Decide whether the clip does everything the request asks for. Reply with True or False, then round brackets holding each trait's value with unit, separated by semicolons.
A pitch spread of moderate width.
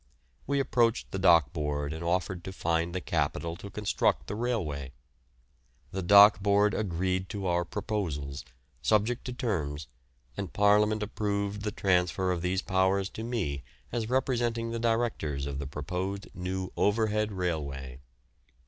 True (4.2 semitones)